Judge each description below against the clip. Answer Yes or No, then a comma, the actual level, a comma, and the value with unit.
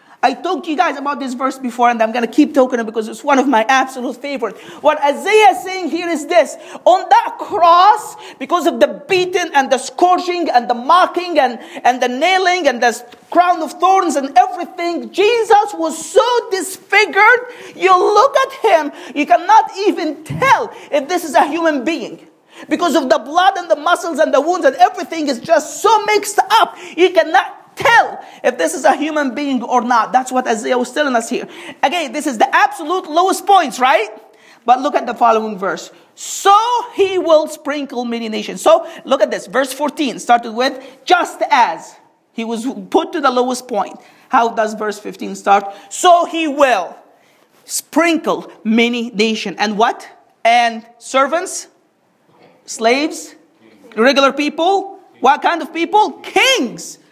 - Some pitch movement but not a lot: No, wide, 6.1 semitones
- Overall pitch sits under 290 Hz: No, very high, 315 Hz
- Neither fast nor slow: Yes, average, 175 wpm